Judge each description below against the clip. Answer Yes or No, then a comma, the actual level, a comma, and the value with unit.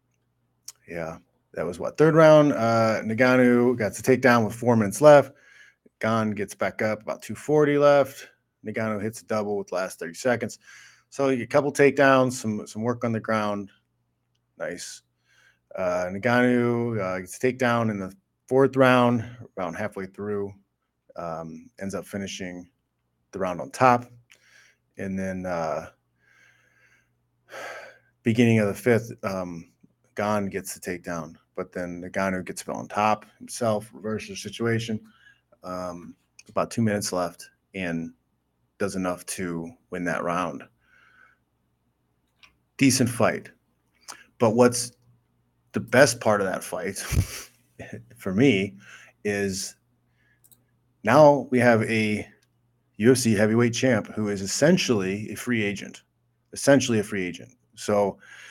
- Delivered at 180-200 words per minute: No, slow, 135 wpm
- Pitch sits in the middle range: No, low, 105 Hz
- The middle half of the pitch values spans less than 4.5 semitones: No, average, 4.8 semitones